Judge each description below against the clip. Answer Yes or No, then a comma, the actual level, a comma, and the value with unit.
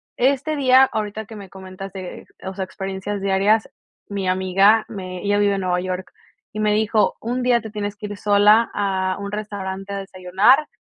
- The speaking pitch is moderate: No, high, 200 Hz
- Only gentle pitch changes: Yes, narrow, 2.1 semitones